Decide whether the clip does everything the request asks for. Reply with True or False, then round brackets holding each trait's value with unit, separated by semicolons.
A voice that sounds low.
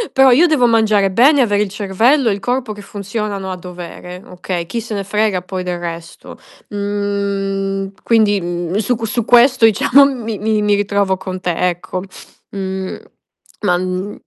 False (200 Hz)